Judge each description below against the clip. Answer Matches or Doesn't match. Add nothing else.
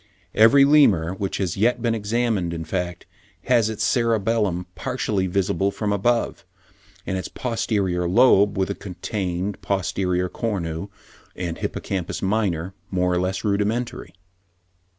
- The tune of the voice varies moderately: Matches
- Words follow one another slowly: Matches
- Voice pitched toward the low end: Matches